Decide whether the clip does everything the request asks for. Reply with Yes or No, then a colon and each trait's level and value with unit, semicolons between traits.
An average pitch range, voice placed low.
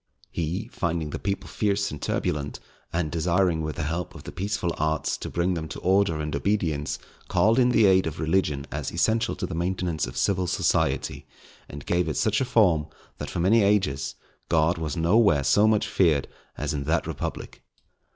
Yes: average, 4.3 semitones; very low, 85 Hz